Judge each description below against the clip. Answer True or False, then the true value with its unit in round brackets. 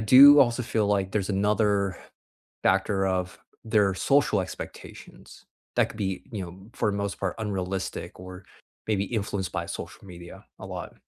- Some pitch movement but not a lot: False (2.2 semitones)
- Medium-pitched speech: False (100 Hz)